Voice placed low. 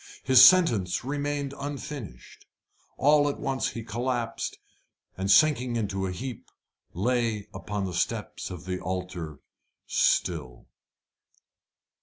Yes: low, 115 Hz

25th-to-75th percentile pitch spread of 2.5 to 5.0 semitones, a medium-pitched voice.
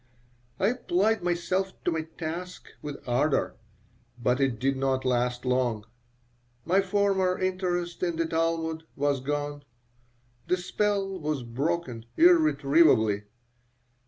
No: wide, 5.6 semitones; medium, 160 Hz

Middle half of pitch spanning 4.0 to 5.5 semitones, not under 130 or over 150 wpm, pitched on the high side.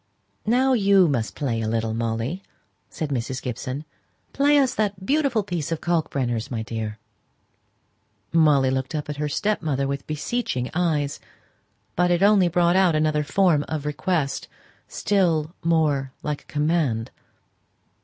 No: average, 5.1 semitones; average, 140 wpm; medium, 150 Hz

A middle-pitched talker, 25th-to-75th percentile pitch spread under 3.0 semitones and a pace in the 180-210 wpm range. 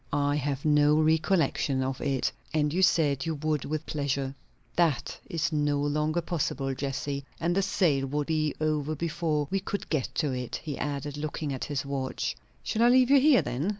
Yes: medium, 150 Hz; narrow, 2.5 semitones; average, 185 wpm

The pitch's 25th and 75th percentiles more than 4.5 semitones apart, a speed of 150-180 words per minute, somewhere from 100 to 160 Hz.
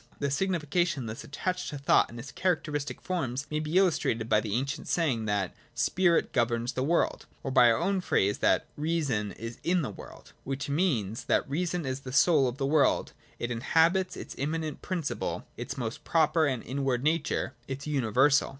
No: average, 5.1 semitones; average, 190 wpm; medium, 140 Hz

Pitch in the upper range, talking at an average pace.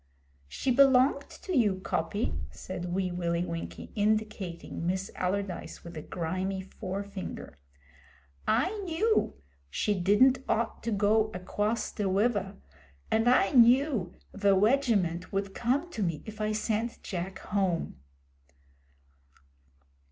No: high, 205 Hz; slow, 120 wpm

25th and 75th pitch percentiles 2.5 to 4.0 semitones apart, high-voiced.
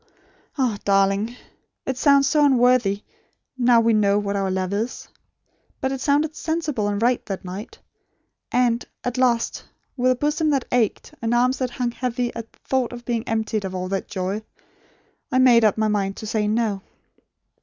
Yes: average, 3.7 semitones; high, 235 Hz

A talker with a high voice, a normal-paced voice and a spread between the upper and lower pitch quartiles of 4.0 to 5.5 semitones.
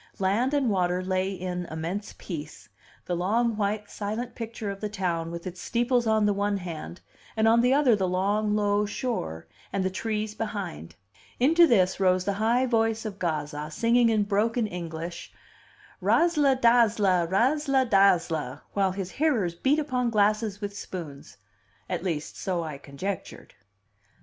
Yes: high, 205 Hz; average, 155 wpm; average, 4.3 semitones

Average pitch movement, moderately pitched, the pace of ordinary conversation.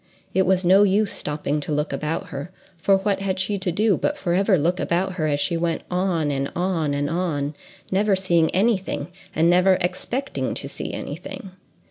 Yes: average, 3.3 semitones; medium, 180 Hz; average, 190 wpm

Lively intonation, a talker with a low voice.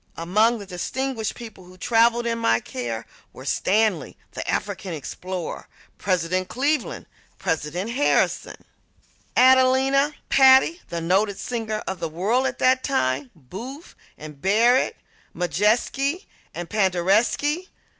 No: wide, 6.5 semitones; high, 215 Hz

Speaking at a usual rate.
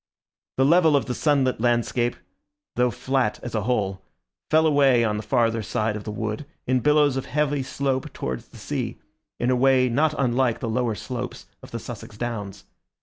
Yes: average, 185 wpm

